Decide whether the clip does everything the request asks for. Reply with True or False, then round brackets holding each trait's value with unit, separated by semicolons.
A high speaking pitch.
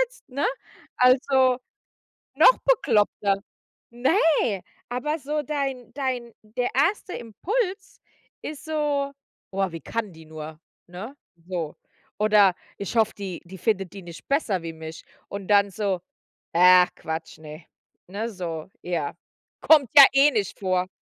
True (215 Hz)